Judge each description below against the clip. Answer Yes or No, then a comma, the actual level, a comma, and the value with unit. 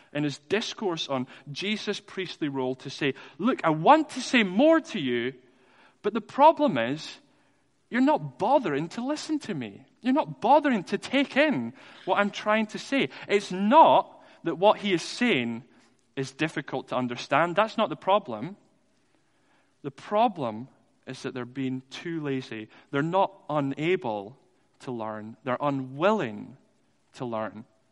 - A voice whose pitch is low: No, medium, 175 Hz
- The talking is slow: No, average, 155 wpm